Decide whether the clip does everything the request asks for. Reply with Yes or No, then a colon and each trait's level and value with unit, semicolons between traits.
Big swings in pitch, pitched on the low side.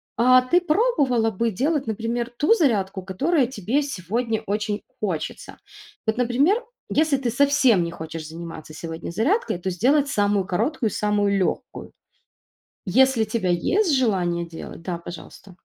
No: wide, 6.8 semitones; high, 225 Hz